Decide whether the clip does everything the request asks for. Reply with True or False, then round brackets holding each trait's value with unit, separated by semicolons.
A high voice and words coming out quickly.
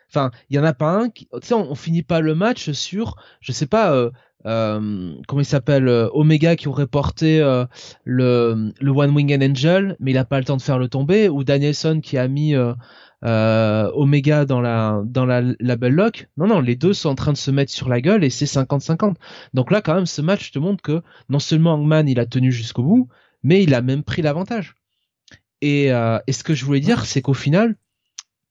False (140 Hz; 235 wpm)